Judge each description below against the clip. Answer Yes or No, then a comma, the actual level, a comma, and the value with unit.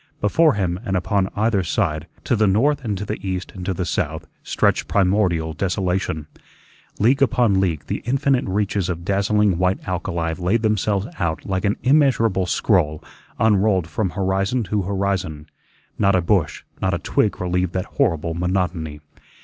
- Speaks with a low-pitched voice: Yes, very low, 95 Hz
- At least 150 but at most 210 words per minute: Yes, average, 160 wpm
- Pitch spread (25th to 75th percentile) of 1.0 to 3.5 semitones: Yes, average, 3.0 semitones